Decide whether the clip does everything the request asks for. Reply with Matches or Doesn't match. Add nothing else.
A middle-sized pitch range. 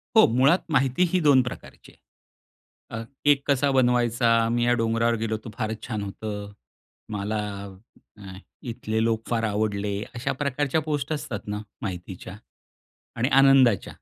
Matches